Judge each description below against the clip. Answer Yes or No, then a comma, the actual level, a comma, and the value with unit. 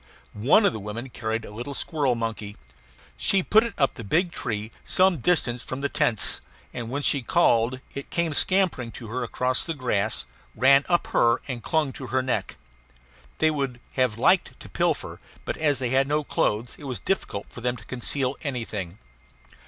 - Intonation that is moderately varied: Yes, average, 4.0 semitones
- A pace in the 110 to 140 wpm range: No, average, 185 wpm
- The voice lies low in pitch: Yes, low, 130 Hz